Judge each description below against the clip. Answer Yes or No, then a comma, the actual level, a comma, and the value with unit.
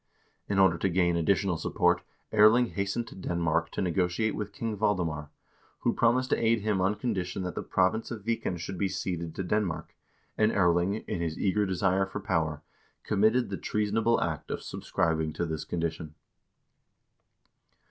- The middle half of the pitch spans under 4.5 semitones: Yes, average, 3.6 semitones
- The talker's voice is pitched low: Yes, very low, 95 Hz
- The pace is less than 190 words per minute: Yes, average, 170 wpm